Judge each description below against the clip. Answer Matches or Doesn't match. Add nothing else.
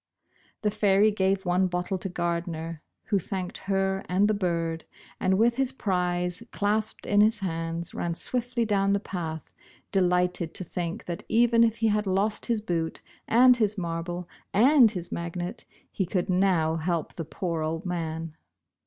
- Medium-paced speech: Matches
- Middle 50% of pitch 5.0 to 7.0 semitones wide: Doesn't match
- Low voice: Doesn't match